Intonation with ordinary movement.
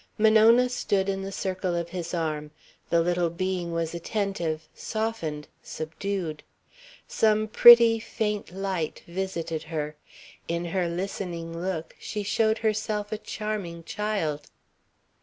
Yes: average, 4.1 semitones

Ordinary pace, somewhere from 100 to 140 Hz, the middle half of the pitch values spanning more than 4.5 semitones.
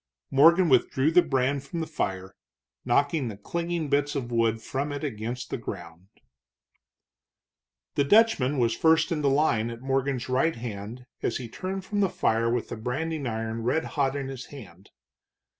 Yes: average, 170 wpm; low, 135 Hz; average, 5.1 semitones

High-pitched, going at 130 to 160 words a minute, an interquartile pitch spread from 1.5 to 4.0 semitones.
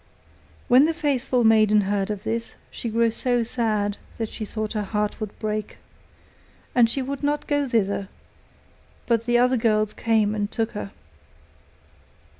Yes: high, 225 Hz; average, 155 wpm; narrow, 2.5 semitones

